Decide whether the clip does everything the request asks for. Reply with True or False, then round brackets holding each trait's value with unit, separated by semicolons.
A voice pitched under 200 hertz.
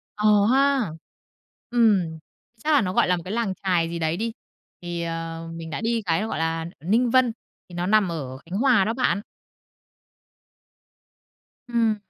True (190 Hz)